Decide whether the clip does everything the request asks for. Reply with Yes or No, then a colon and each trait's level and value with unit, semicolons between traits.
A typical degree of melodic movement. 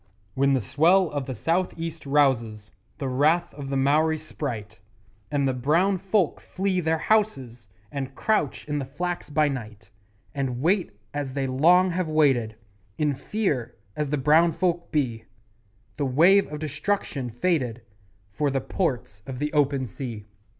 Yes: average, 4.2 semitones